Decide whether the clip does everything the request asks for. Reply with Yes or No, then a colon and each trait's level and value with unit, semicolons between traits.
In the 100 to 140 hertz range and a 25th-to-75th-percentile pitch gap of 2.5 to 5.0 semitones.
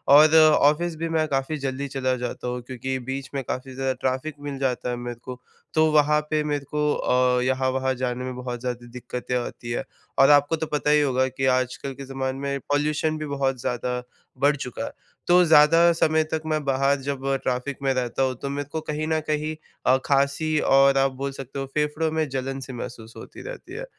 Yes: low, 135 Hz; average, 2.8 semitones